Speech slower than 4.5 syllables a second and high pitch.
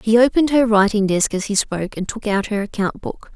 No: 5.8 syllables/s; high, 215 Hz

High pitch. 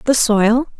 Yes: high, 235 Hz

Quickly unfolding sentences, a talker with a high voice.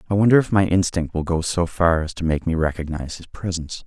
No: fast, 250 wpm; very low, 85 Hz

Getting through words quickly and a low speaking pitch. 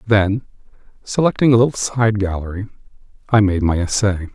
No: average, 140 wpm; low, 105 Hz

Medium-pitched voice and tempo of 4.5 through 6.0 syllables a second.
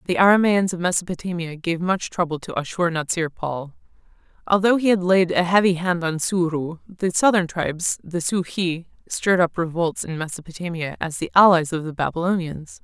Yes: medium, 175 Hz; 5.3 syllables/s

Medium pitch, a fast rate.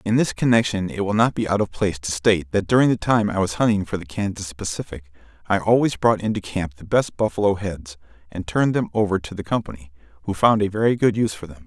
No: very low, 95 Hz; fast, 240 wpm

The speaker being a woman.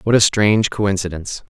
No: male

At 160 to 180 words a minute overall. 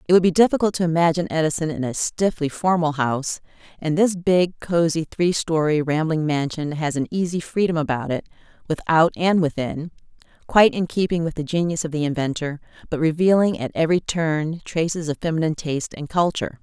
Yes: average, 175 wpm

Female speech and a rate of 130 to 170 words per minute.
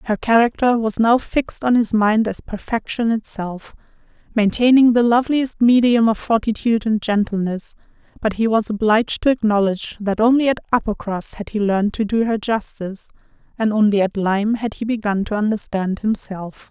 Yes: female; average, 165 wpm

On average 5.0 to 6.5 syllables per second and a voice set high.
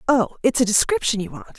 Yes: 6.3 syllables/s; high, 235 Hz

